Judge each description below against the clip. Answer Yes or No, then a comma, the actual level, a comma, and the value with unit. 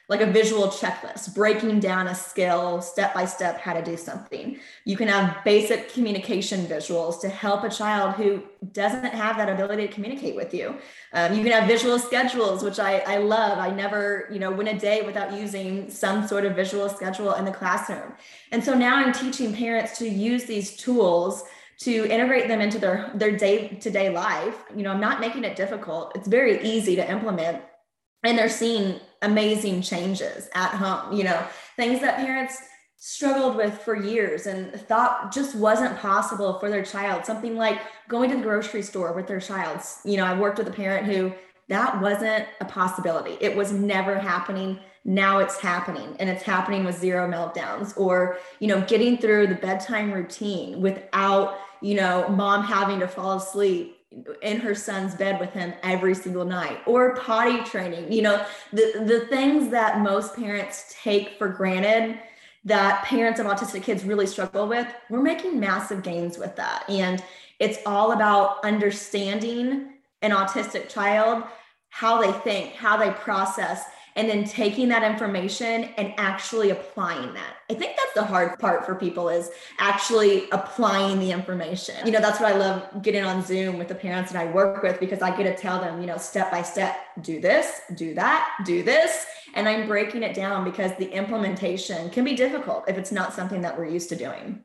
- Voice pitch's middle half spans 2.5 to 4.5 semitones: Yes, average, 2.8 semitones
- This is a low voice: No, high, 200 Hz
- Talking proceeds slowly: No, average, 185 wpm